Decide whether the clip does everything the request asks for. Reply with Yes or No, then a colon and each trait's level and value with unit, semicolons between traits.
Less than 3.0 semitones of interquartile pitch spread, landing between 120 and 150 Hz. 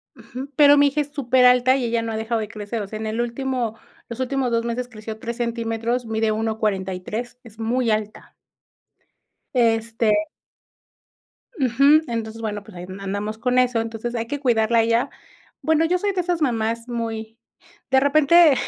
No: narrow, 2.6 semitones; high, 230 Hz